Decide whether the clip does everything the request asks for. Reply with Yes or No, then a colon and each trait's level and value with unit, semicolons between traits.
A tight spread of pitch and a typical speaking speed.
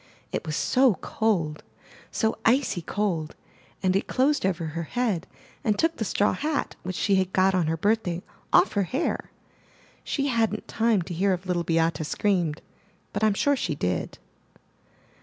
No: average, 4.8 semitones; average, 165 wpm